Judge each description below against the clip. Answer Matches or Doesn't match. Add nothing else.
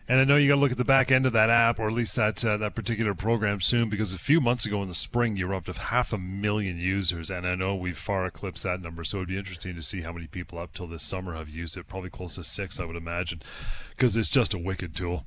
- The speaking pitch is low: Matches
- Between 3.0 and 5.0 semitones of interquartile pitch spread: Matches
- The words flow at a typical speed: Doesn't match